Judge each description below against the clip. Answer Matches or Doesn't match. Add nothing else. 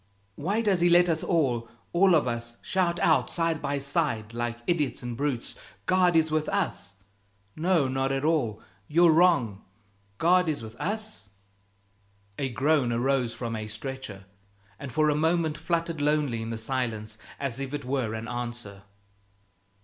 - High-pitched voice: Doesn't match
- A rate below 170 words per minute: Matches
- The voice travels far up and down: Matches